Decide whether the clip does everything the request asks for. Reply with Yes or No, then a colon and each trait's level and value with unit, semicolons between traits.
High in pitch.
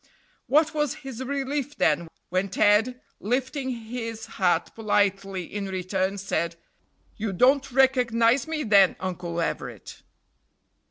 Yes: high, 225 Hz